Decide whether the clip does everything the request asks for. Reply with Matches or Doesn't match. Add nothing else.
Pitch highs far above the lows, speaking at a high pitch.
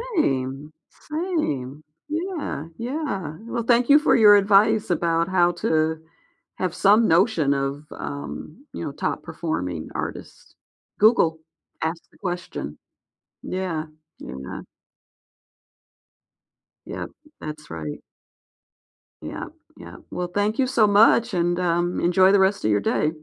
Doesn't match